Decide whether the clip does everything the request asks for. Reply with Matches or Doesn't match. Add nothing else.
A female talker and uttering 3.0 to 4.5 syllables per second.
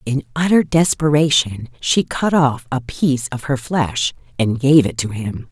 Matches